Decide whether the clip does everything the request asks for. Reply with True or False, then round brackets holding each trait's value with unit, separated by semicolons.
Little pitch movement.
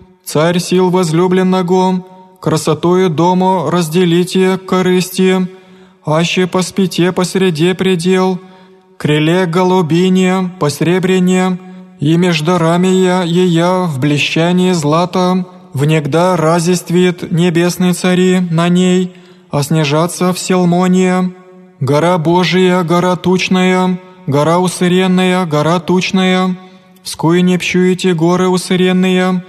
True (1.1 semitones)